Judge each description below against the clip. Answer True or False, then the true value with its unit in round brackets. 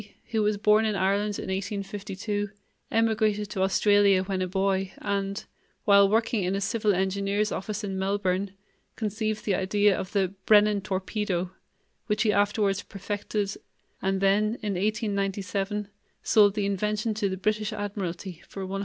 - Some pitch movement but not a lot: False (1.5 semitones)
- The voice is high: True (200 Hz)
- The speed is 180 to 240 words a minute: False (155 wpm)